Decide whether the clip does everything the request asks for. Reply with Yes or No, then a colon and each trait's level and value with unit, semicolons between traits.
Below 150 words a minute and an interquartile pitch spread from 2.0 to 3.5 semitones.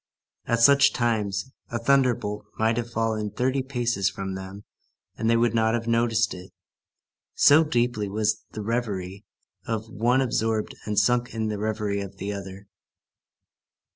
No: average, 155 wpm; narrow, 2.6 semitones